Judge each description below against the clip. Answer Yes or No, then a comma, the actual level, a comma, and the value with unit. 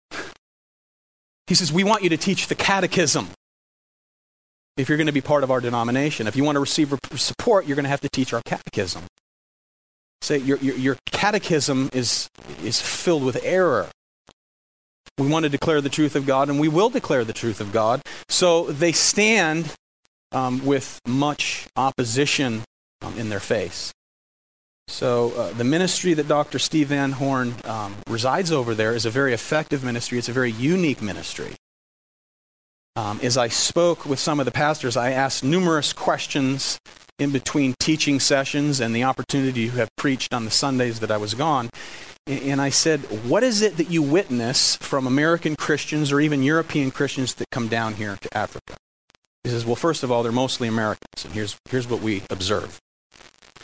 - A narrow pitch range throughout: No, average, 4.2 semitones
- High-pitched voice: No, low, 135 Hz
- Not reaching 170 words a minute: No, average, 180 wpm